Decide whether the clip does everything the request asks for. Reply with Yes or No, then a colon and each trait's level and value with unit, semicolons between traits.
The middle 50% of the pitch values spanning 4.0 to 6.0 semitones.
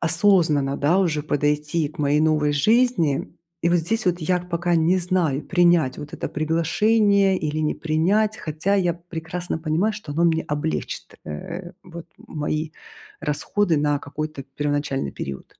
No: average, 3.2 semitones